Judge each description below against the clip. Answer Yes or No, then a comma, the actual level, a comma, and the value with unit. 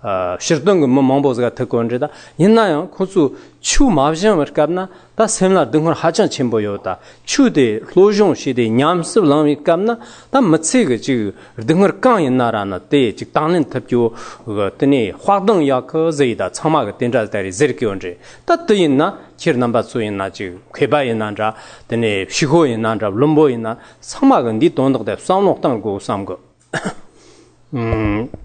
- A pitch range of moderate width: No, wide, 7.7 semitones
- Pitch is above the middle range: No, medium, 140 Hz